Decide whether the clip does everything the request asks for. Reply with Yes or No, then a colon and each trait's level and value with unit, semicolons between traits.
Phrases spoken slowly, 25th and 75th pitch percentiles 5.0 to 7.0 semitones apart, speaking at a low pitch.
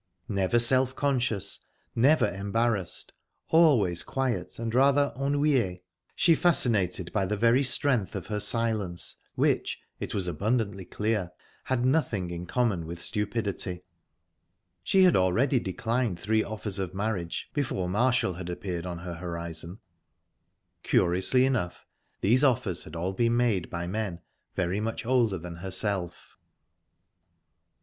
Yes: slow, 130 wpm; average, 5.3 semitones; low, 105 Hz